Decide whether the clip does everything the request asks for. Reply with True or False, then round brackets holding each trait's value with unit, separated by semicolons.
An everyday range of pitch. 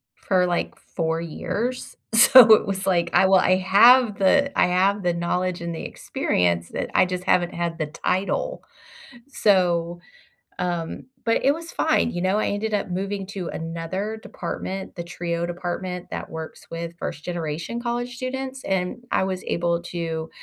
True (3.5 semitones)